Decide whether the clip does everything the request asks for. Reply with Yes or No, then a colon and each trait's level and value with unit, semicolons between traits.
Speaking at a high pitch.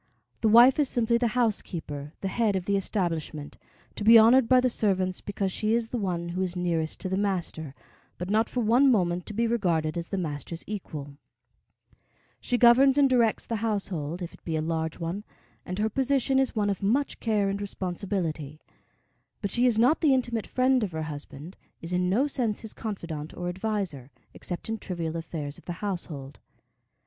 Yes: high, 195 Hz